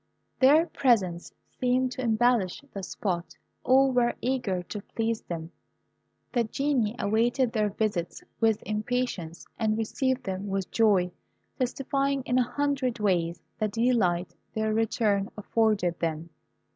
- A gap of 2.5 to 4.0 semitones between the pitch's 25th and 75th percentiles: No, average, 4.5 semitones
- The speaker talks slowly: Yes, slow, 130 wpm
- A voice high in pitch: Yes, high, 220 Hz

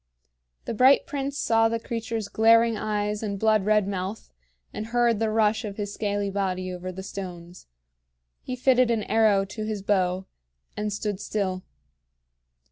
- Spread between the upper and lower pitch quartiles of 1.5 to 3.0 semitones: Yes, narrow, 2.4 semitones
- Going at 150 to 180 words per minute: Yes, average, 155 wpm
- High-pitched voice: Yes, high, 210 Hz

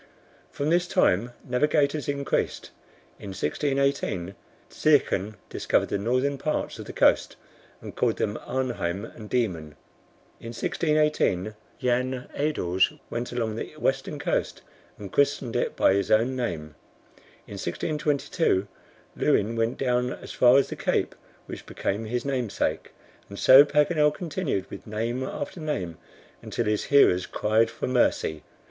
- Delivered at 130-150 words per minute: Yes, slow, 135 wpm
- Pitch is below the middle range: Yes, low, 125 Hz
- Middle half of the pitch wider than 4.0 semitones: Yes, wide, 5.4 semitones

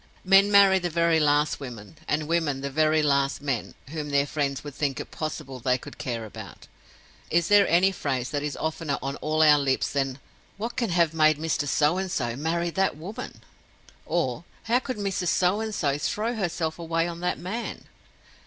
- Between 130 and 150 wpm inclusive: No, average, 190 wpm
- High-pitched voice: No, medium, 155 Hz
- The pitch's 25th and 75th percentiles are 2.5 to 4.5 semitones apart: Yes, average, 4.0 semitones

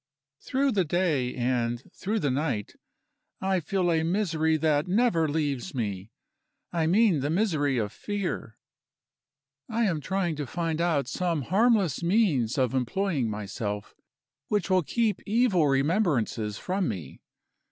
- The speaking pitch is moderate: Yes, medium, 160 Hz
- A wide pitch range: Yes, wide, 6.7 semitones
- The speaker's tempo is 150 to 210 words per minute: No, slow, 135 wpm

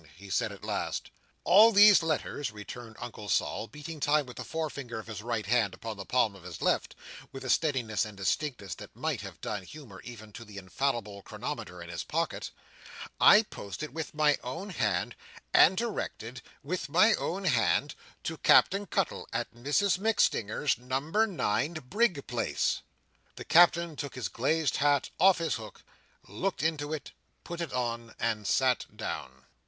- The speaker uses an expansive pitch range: Yes, wide, 6.8 semitones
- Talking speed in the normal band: Yes, average, 170 wpm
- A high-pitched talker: No, low, 135 Hz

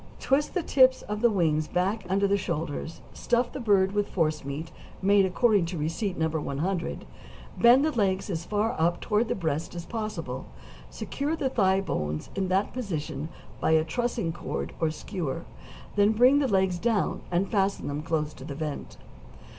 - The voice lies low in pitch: No, high, 190 Hz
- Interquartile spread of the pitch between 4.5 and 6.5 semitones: Yes, average, 5.2 semitones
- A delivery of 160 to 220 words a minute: Yes, average, 175 wpm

